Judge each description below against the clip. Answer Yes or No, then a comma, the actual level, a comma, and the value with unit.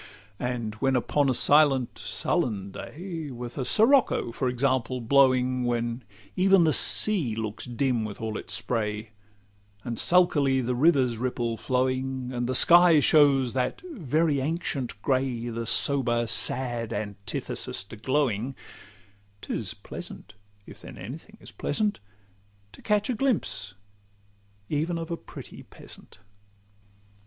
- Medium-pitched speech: No, low, 130 Hz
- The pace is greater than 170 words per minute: No, slow, 135 wpm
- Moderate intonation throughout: Yes, average, 4.0 semitones